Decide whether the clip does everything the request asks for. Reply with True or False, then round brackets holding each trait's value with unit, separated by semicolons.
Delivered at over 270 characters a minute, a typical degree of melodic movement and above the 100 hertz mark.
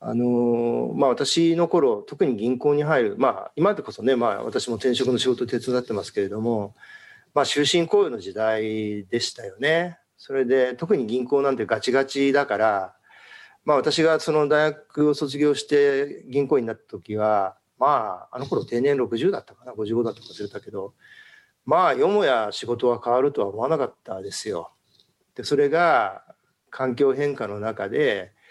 True (310 characters per minute; 4.1 semitones; 130 Hz)